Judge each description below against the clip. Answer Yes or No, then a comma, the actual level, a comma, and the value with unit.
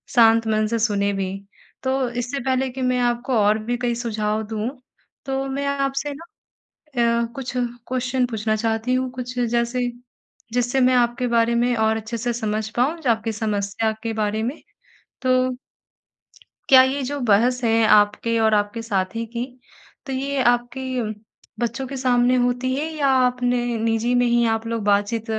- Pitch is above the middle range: Yes, high, 240 Hz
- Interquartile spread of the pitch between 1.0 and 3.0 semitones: Yes, narrow, 2.4 semitones